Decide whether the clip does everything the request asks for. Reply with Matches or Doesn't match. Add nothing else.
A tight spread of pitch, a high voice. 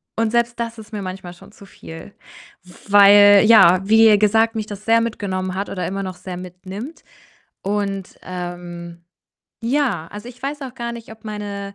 Doesn't match